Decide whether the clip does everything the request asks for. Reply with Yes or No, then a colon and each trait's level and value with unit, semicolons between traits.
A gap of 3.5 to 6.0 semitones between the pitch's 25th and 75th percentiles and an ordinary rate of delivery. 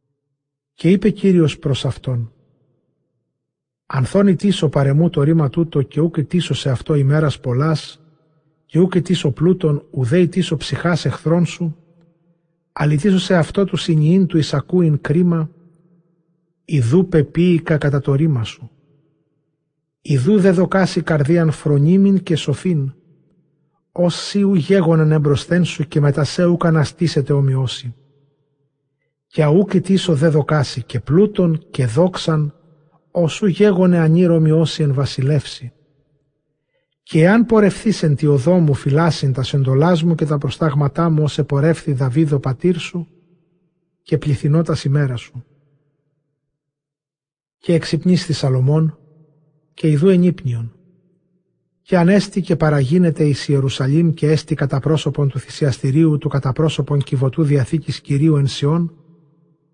No: average, 2.9 semitones; average, 125 wpm